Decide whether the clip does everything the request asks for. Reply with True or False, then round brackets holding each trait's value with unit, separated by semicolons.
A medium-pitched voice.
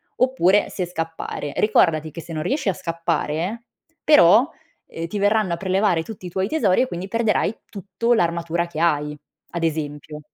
True (175 Hz)